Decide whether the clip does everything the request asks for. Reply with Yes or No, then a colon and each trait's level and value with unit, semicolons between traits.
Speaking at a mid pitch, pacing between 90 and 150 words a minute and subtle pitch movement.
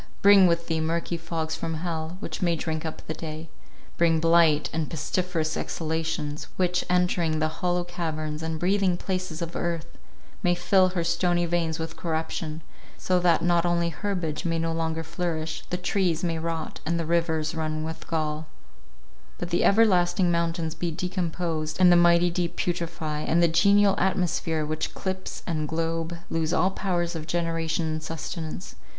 No: medium, 165 Hz; average, 165 wpm; narrow, 1.7 semitones